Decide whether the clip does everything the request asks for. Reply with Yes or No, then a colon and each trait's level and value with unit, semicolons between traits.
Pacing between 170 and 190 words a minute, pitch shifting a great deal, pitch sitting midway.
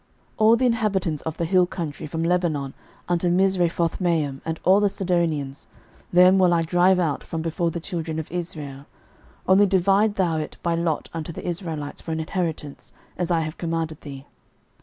No: average, 180 wpm; narrow, 2.5 semitones; medium, 170 Hz